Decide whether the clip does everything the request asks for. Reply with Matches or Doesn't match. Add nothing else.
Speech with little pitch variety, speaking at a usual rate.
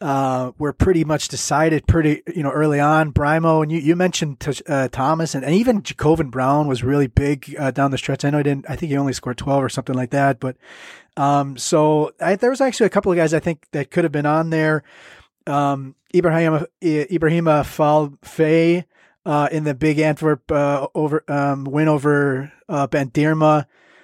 Matches